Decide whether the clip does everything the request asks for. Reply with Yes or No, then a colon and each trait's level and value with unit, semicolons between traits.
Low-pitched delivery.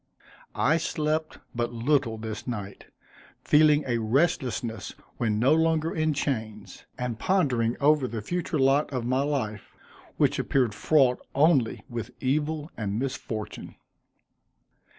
Yes: low, 130 Hz